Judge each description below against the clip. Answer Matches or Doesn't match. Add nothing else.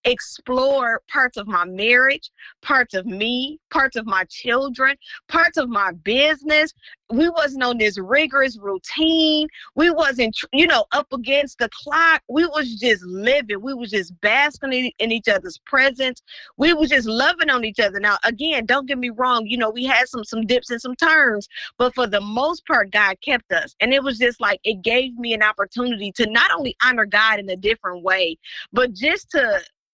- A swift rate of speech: Doesn't match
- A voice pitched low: Doesn't match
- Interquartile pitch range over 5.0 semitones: Doesn't match